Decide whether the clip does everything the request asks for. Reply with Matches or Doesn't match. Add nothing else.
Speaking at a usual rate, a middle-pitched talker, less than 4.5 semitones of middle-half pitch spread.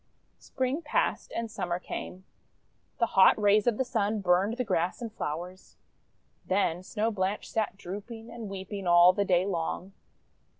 Doesn't match